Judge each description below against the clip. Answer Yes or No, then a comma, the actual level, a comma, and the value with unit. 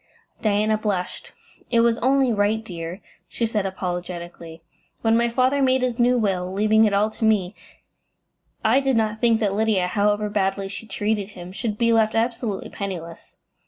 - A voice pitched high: Yes, high, 215 Hz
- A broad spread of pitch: No, average, 3.0 semitones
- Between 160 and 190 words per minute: Yes, average, 165 wpm